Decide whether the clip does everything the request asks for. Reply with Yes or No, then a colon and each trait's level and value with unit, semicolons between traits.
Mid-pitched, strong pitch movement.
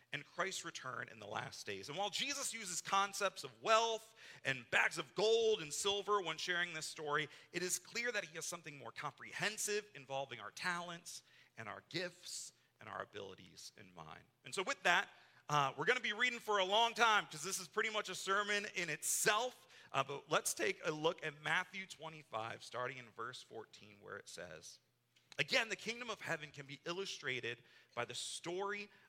Yes: medium, 180 Hz; wide, 5.7 semitones